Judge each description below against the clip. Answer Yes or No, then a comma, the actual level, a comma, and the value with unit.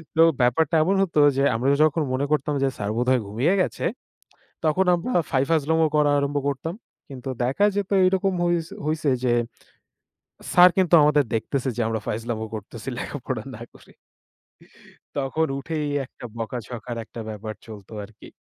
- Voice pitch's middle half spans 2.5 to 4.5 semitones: No, wide, 5.5 semitones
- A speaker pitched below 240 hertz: Yes, medium, 140 Hz